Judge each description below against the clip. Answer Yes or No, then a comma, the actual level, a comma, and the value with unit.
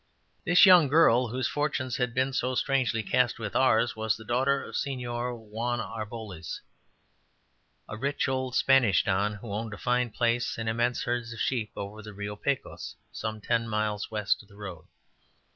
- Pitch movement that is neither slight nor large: Yes, average, 3.0 semitones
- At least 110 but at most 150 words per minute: No, average, 175 wpm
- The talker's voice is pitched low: Yes, low, 115 Hz